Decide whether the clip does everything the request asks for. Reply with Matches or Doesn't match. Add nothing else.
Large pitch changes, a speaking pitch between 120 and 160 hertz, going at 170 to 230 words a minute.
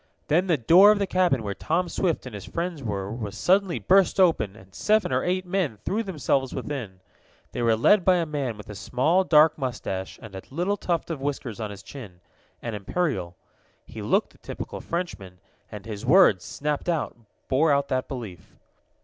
Matches